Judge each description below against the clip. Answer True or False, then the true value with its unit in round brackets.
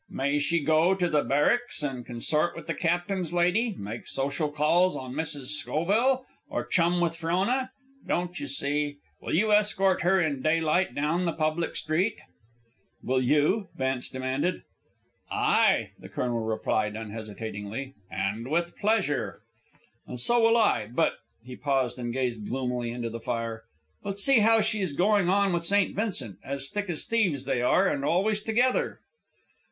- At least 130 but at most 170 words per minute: True (165 wpm)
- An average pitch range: False (6.7 semitones)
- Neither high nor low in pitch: True (155 Hz)